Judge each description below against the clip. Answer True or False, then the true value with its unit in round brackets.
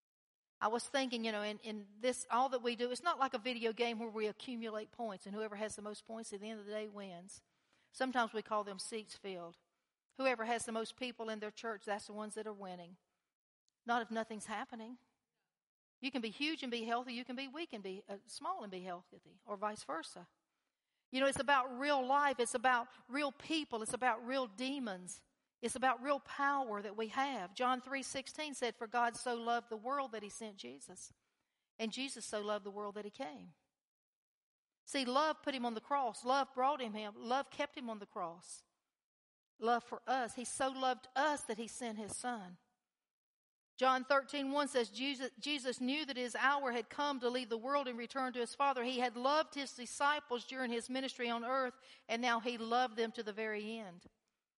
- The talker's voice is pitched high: True (240 Hz)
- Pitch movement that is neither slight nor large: True (3.4 semitones)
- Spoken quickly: True (210 wpm)